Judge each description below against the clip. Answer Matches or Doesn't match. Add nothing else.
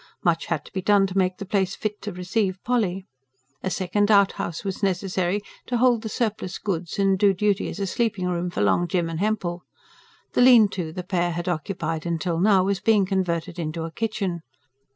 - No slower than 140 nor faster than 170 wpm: Doesn't match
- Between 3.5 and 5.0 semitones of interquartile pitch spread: Doesn't match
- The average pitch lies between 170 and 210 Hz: Matches